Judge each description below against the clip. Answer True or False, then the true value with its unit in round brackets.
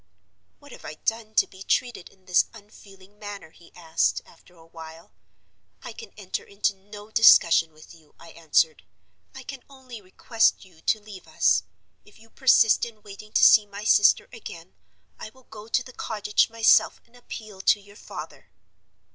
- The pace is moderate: True (175 wpm)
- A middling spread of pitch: True (3.9 semitones)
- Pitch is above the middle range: True (205 Hz)